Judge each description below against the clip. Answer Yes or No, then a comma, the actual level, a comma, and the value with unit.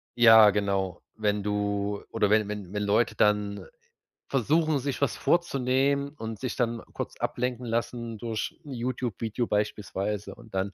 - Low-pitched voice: Yes, low, 110 Hz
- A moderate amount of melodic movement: Yes, average, 3.3 semitones